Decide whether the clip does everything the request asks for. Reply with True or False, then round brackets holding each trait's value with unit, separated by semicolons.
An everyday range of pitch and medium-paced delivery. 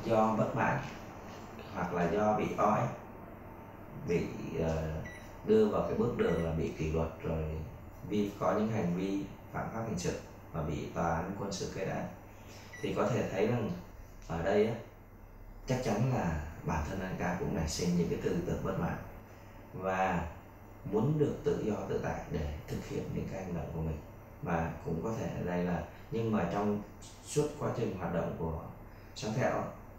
True (4.3 semitones; 185 wpm)